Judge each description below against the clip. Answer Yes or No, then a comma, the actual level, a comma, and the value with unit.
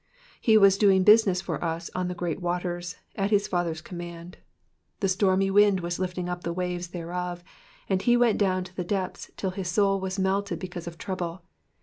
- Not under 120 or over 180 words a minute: No, average, 195 wpm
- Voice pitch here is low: No, medium, 185 Hz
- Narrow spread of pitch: Yes, narrow, 1.9 semitones